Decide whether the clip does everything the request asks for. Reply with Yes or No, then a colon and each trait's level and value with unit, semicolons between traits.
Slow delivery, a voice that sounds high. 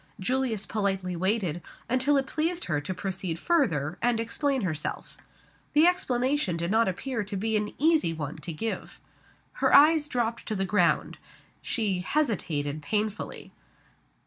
No: average, 145 wpm; high, 215 Hz